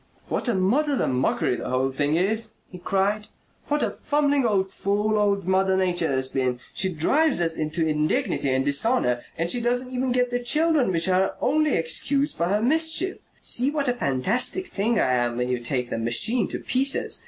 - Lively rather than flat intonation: Yes, wide, 8.7 semitones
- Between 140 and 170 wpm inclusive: No, average, 200 wpm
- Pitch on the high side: Yes, high, 195 Hz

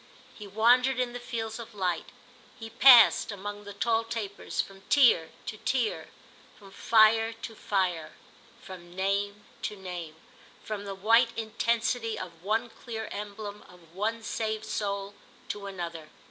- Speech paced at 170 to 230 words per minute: No, average, 145 wpm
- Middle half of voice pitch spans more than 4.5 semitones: No, average, 2.8 semitones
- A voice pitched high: Yes, high, 210 Hz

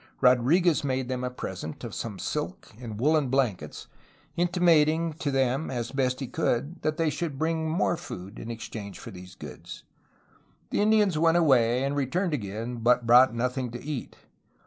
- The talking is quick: No, average, 170 wpm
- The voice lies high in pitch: No, low, 135 Hz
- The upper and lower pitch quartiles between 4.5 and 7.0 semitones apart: Yes, average, 5.0 semitones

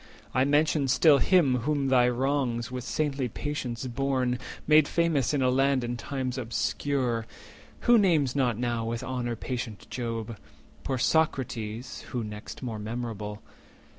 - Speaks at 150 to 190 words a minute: No, average, 140 wpm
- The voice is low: Yes, low, 125 Hz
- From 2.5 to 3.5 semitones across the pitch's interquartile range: Yes, average, 2.9 semitones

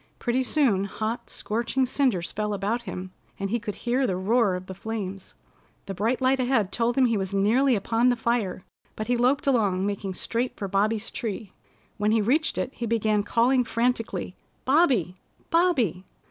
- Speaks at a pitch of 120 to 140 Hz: No, high, 225 Hz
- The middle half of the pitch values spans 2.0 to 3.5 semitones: No, average, 3.9 semitones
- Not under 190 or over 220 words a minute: No, average, 175 wpm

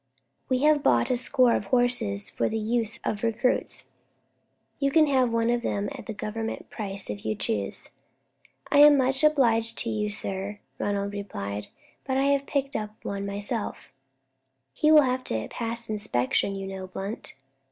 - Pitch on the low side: No, high, 225 Hz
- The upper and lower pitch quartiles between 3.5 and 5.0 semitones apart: Yes, average, 4.4 semitones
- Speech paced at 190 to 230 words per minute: No, average, 165 wpm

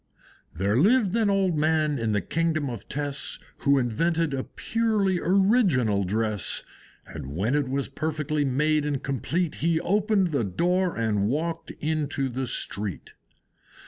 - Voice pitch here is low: No, medium, 150 Hz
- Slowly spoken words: No, average, 145 wpm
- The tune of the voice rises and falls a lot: Yes, wide, 5.9 semitones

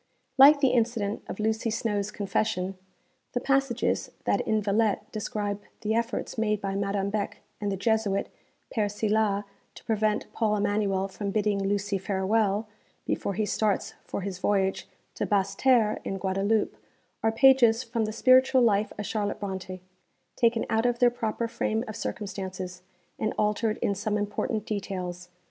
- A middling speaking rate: Yes, average, 155 wpm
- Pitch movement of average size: No, narrow, 2.1 semitones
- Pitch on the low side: No, high, 210 Hz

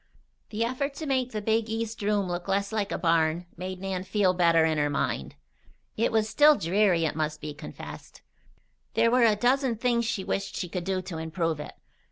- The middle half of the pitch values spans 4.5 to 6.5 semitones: Yes, average, 5.1 semitones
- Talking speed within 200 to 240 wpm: Yes, fast, 205 wpm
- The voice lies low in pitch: No, high, 195 Hz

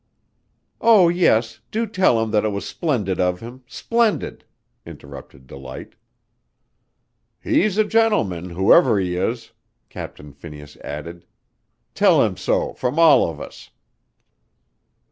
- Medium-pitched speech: No, low, 110 Hz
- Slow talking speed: Yes, slow, 120 wpm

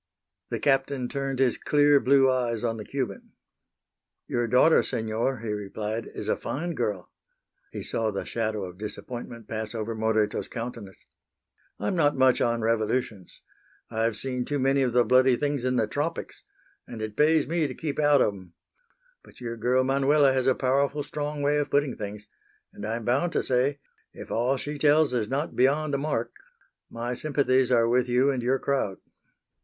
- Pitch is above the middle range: No, low, 125 Hz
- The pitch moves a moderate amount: Yes, average, 3.8 semitones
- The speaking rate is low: No, average, 180 wpm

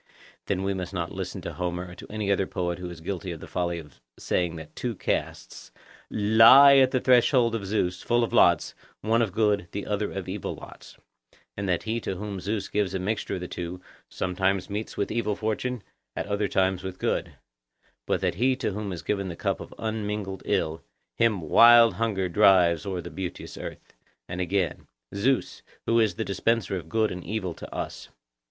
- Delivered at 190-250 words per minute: Yes, average, 200 wpm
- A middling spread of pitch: Yes, average, 3.4 semitones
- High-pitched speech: No, low, 100 Hz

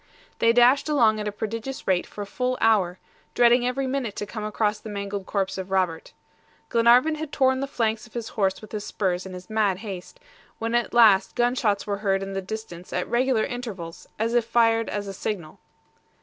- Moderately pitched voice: No, high, 220 Hz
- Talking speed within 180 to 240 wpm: Yes, fast, 205 wpm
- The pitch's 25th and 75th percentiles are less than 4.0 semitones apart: Yes, average, 3.6 semitones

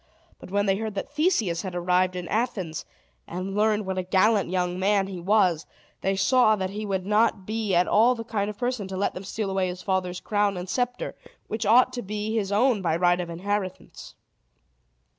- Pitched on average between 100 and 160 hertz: No, high, 195 Hz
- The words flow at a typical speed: No, fast, 210 wpm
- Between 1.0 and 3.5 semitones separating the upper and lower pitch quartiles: Yes, average, 2.8 semitones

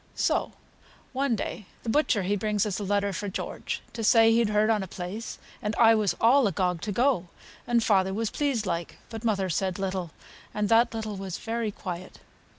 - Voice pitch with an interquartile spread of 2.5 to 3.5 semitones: Yes, average, 3.0 semitones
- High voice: Yes, high, 210 Hz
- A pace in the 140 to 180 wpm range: No, average, 195 wpm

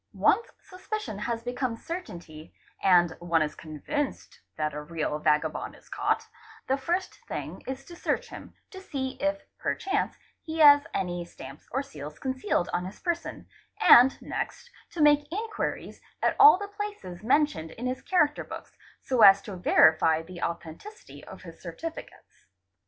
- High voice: Yes, very high, 255 Hz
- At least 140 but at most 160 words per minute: Yes, average, 155 wpm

